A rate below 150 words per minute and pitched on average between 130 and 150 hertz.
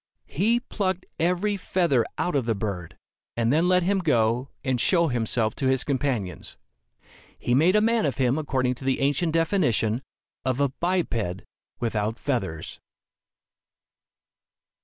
Yes: average, 140 wpm; low, 135 Hz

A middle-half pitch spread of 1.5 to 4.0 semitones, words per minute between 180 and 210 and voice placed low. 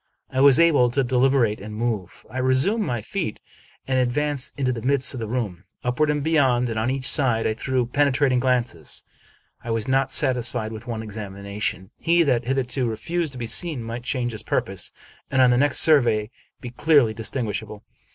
Yes: average, 3.3 semitones; average, 185 wpm; low, 125 Hz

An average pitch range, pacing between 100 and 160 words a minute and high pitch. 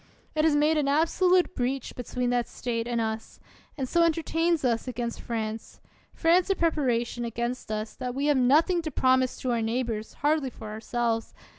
No: average, 4.8 semitones; average, 175 wpm; very high, 255 Hz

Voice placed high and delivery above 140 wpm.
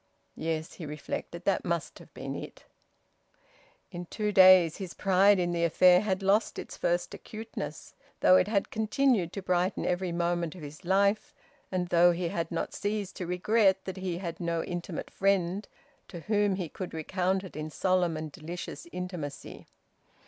No: medium, 180 Hz; average, 170 wpm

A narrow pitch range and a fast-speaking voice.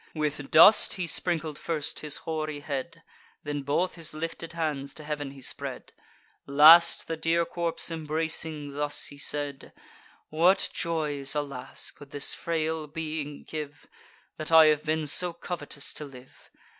No: narrow, 2.1 semitones; average, 145 wpm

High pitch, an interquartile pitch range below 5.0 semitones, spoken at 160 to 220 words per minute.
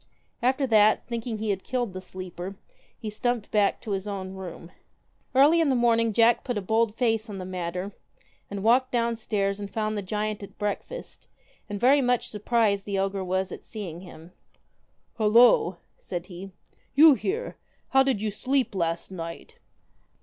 Yes: high, 210 Hz; average, 3.8 semitones; average, 180 wpm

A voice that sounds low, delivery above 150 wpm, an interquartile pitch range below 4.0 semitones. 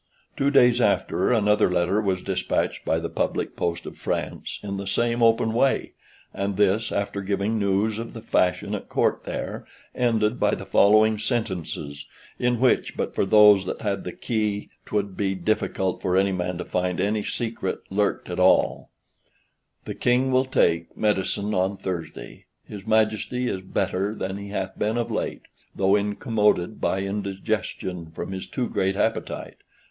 Yes: low, 100 Hz; average, 165 wpm; average, 2.7 semitones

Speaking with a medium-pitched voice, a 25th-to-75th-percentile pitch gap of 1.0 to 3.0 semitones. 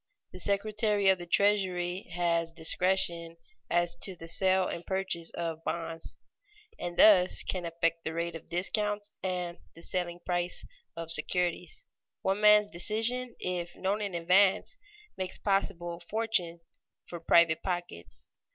Yes: medium, 180 Hz; narrow, 2.4 semitones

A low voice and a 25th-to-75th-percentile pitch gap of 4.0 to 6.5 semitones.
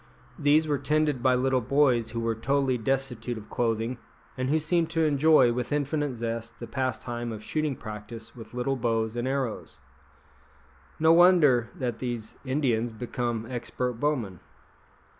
No: low, 125 Hz; average, 3.6 semitones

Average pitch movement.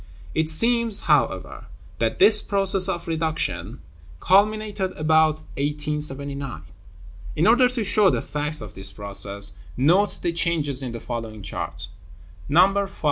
No: wide, 7.6 semitones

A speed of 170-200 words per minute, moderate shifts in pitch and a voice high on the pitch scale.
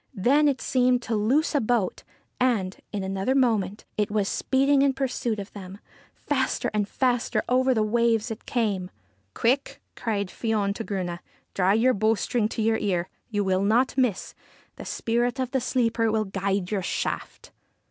Yes: average, 180 wpm; average, 4.0 semitones; high, 220 Hz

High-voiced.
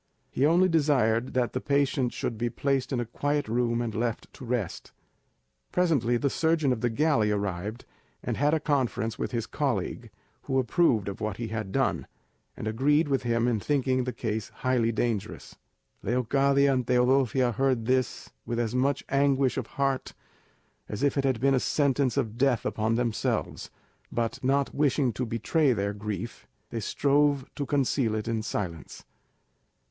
No: low, 125 Hz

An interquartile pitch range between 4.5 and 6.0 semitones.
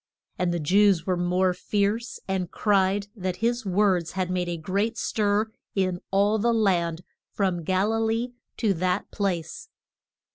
No: average, 2.8 semitones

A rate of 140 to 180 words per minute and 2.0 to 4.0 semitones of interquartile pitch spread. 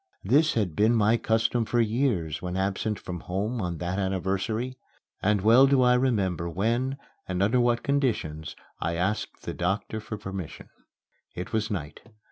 No: average, 160 wpm; average, 4.6 semitones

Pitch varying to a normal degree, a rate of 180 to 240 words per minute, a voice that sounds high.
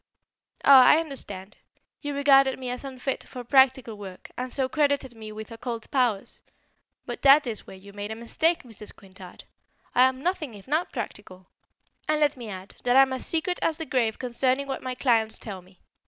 Yes: average, 4.2 semitones; average, 185 wpm; very high, 255 Hz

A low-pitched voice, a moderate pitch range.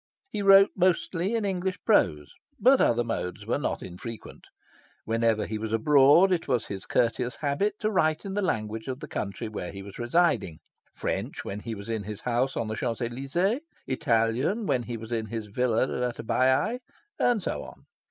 No: low, 125 Hz; wide, 8.0 semitones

